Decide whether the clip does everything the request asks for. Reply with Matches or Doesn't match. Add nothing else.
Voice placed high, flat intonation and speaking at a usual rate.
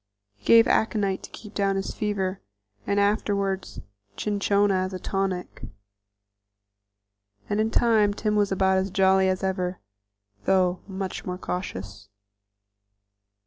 Doesn't match